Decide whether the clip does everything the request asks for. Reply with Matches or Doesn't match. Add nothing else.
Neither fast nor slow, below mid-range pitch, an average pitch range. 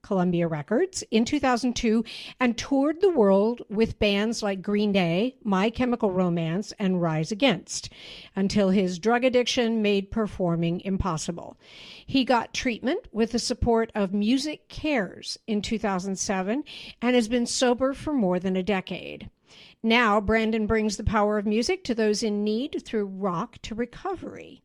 Doesn't match